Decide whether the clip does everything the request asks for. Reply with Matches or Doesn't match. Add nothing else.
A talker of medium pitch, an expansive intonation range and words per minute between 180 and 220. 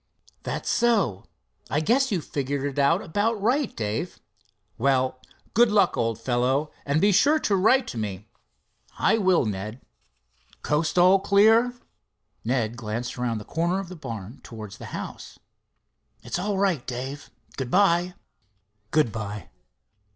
Doesn't match